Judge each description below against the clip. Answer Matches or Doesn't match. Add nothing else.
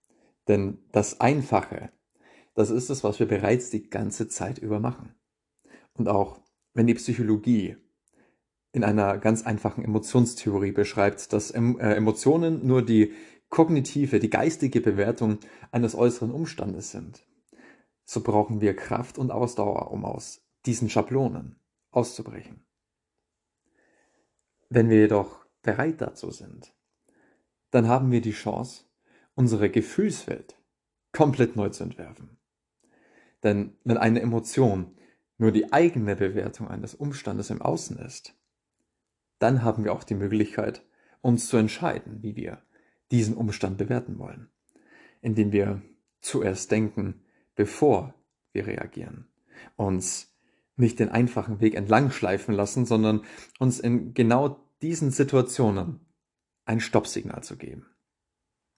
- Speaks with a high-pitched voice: Doesn't match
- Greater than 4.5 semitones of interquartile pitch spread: Doesn't match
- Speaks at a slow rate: Matches